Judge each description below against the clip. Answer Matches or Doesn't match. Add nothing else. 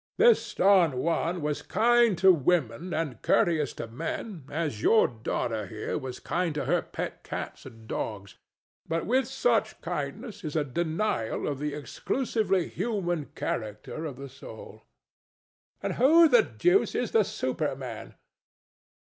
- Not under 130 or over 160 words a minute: Matches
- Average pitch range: Doesn't match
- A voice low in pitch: Doesn't match